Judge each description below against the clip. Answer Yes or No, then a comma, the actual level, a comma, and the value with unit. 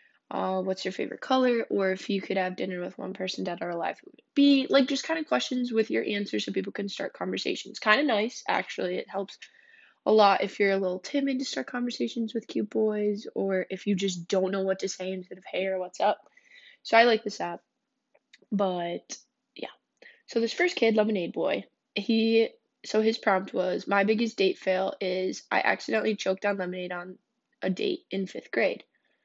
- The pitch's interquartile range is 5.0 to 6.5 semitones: Yes, wide, 5.6 semitones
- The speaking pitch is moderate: No, high, 210 Hz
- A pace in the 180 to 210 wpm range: Yes, fast, 205 wpm